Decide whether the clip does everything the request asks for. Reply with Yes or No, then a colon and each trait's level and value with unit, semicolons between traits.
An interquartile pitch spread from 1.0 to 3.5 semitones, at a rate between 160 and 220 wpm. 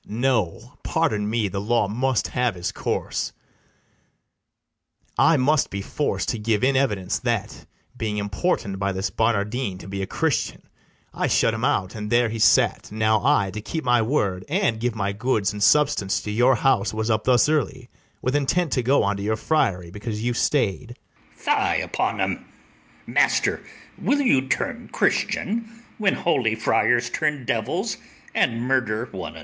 No: average, 4.3 semitones; average, 170 wpm